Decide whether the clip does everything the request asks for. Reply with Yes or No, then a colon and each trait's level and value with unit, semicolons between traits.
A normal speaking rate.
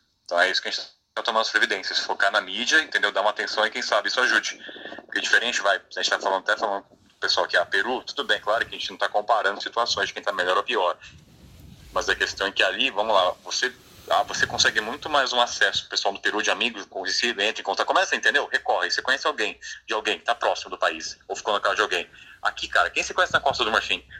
No: fast, 270 wpm